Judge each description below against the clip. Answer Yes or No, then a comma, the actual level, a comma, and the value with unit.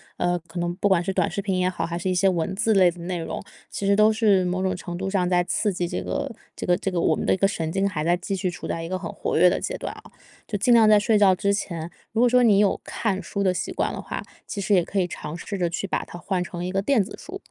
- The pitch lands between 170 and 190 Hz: Yes, medium, 185 Hz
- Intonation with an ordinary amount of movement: No, narrow, 2.2 semitones